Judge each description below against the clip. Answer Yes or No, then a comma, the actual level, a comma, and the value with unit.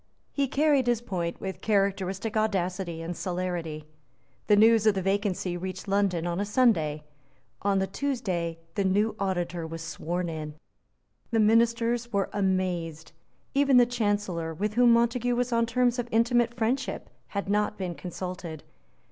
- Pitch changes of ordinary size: Yes, average, 4.7 semitones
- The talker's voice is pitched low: No, high, 200 Hz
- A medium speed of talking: Yes, average, 150 wpm